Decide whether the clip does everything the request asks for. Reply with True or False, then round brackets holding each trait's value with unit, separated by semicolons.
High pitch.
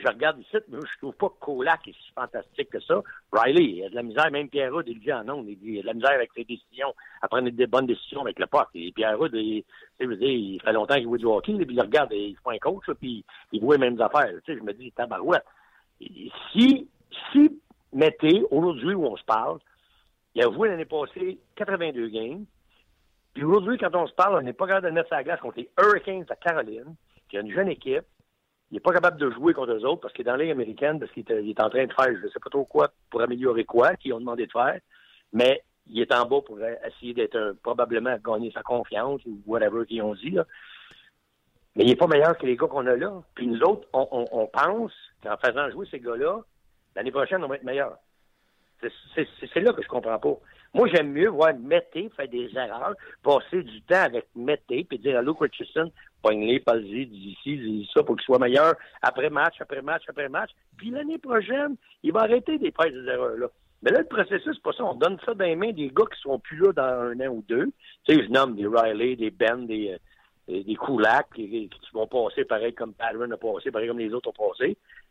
True (195 Hz)